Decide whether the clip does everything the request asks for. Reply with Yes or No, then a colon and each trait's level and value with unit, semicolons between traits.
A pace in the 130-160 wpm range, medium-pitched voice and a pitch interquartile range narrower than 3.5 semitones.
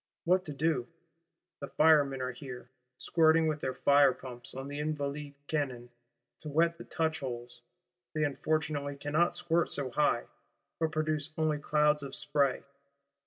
Yes: average, 145 wpm; medium, 145 Hz; narrow, 2.5 semitones